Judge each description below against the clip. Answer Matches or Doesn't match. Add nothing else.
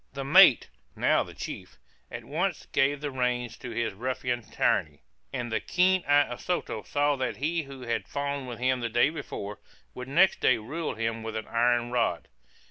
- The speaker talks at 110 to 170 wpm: Doesn't match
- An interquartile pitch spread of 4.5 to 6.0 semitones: Doesn't match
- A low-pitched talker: Matches